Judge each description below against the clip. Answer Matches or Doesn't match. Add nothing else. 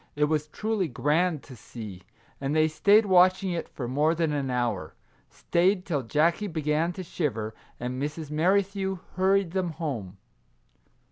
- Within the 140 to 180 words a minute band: Matches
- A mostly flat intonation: Doesn't match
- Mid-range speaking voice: Matches